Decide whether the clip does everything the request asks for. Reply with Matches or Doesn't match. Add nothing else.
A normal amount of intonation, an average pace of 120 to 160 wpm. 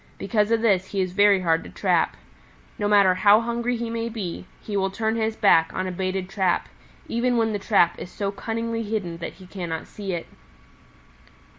Doesn't match